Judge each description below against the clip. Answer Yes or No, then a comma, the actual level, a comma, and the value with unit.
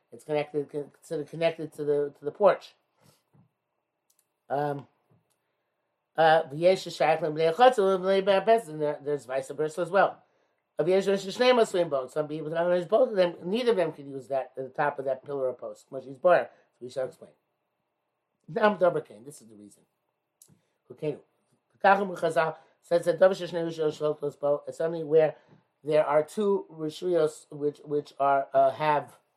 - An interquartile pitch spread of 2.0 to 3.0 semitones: No, average, 3.4 semitones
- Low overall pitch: No, medium, 155 Hz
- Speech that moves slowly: Yes, slow, 110 wpm